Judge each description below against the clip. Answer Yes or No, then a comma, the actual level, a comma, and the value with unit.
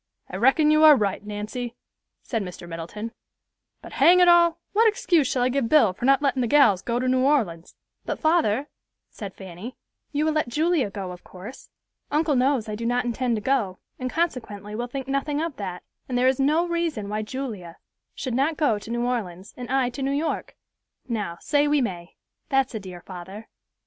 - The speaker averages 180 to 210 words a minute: Yes, average, 200 wpm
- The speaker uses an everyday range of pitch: No, wide, 5.8 semitones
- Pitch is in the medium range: No, very high, 250 Hz